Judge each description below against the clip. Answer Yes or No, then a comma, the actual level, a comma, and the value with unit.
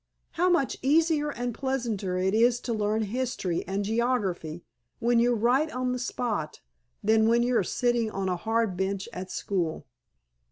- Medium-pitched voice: No, high, 230 Hz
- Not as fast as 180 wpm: Yes, average, 165 wpm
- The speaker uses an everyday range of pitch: Yes, average, 4.2 semitones